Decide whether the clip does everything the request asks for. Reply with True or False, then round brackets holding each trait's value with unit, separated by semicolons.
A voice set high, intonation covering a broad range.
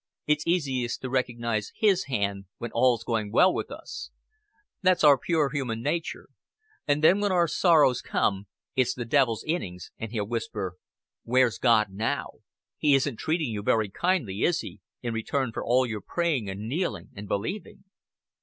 False (125 Hz; 5.8 semitones)